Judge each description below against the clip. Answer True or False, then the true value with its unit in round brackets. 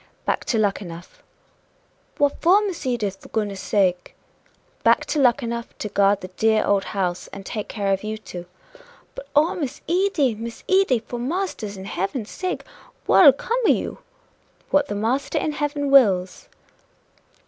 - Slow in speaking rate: False (160 wpm)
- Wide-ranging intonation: True (6.6 semitones)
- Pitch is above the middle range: True (230 Hz)